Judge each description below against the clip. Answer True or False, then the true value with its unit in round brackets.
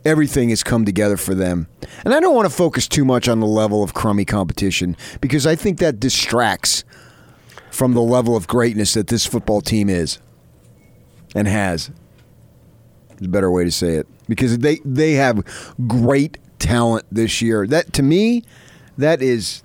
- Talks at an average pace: True (175 wpm)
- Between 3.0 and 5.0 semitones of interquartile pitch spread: True (4.4 semitones)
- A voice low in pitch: True (115 Hz)